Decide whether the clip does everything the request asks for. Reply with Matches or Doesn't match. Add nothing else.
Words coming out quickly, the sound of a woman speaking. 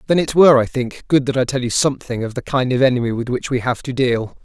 Doesn't match